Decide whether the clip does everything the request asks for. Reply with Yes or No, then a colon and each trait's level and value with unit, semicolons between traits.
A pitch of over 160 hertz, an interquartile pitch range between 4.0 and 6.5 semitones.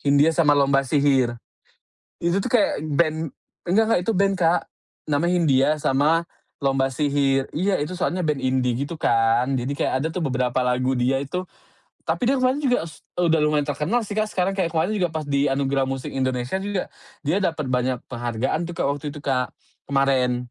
No: medium, 145 Hz; average, 4.7 semitones